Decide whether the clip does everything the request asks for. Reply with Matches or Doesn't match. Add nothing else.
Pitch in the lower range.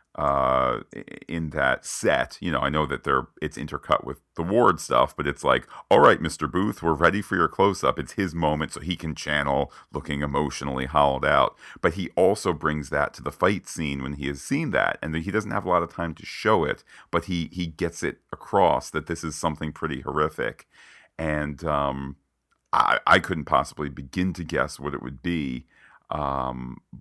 Matches